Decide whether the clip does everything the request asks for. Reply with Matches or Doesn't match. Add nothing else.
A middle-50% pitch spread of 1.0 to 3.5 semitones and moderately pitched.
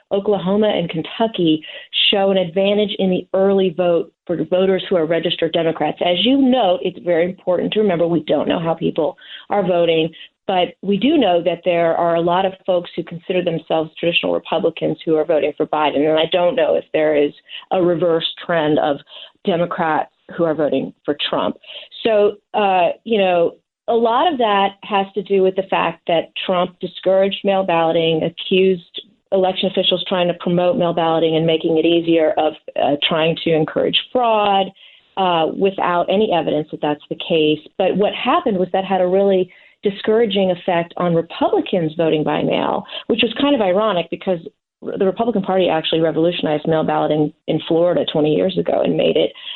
Matches